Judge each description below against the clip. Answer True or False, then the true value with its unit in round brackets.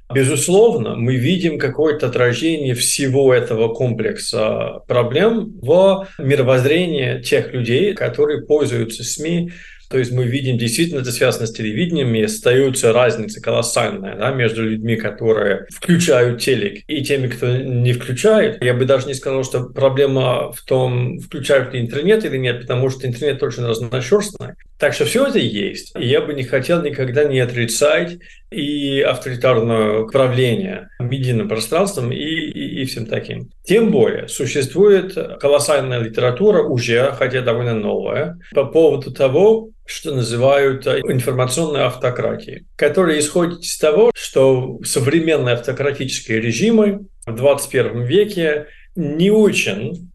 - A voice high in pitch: False (135 Hz)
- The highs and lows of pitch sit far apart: False (4.4 semitones)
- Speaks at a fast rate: False (130 wpm)